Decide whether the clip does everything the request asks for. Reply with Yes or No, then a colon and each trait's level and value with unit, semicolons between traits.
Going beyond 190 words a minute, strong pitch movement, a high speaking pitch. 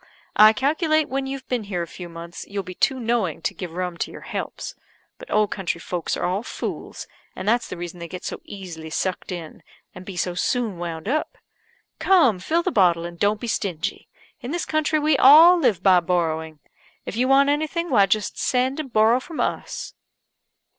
Yes: average, 200 wpm; wide, 7.2 semitones; high, 205 Hz